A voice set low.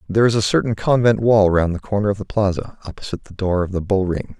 Yes: low, 100 Hz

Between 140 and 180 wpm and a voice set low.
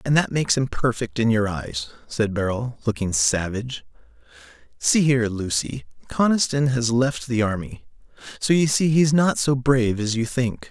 Yes: average, 170 wpm; low, 120 Hz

